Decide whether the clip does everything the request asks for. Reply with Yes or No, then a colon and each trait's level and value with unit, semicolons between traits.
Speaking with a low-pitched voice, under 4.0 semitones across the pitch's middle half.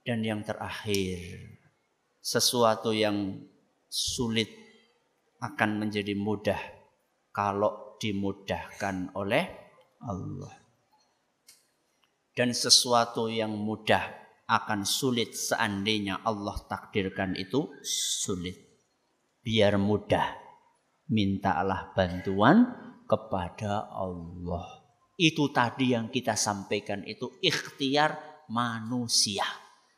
Yes: low, 105 Hz; average, 3.5 semitones